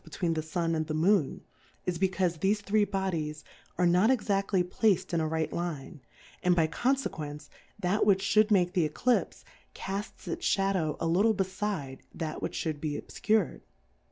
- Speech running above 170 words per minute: Yes, average, 180 wpm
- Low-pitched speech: No, medium, 180 Hz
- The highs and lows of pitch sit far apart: No, average, 3.9 semitones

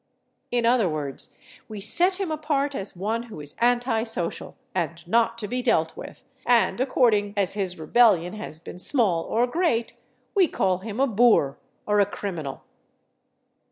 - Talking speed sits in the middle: Yes, average, 160 wpm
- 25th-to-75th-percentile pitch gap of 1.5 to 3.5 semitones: No, average, 5.2 semitones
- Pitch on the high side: Yes, high, 220 Hz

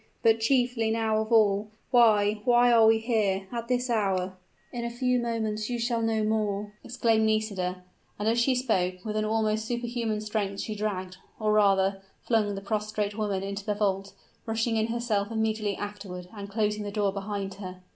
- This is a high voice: Yes, high, 215 Hz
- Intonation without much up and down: Yes, narrow, 2.1 semitones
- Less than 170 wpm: No, average, 180 wpm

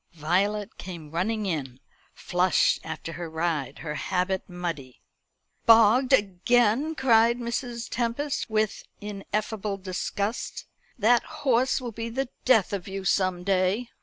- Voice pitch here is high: Yes, high, 205 Hz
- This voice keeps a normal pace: No, slow, 125 wpm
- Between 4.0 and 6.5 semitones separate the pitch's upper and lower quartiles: Yes, average, 4.8 semitones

